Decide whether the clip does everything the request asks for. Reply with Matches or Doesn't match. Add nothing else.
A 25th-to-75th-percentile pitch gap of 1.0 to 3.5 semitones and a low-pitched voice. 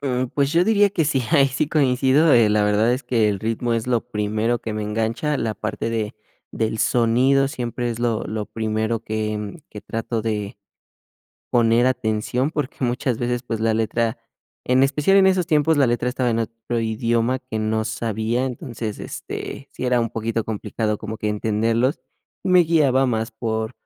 Matches